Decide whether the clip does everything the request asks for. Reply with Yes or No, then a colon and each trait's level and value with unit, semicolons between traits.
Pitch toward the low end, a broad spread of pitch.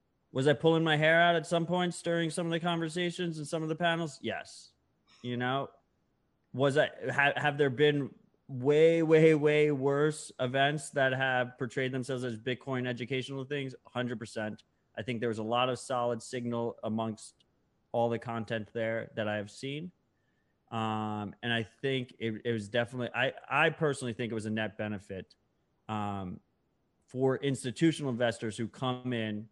No: low, 130 Hz; average, 4.6 semitones